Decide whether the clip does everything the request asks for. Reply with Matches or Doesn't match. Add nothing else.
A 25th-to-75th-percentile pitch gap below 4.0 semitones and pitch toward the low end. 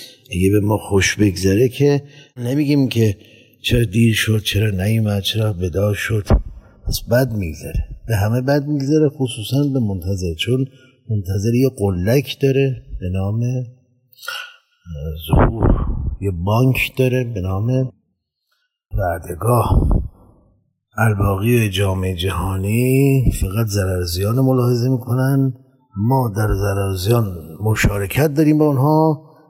Doesn't match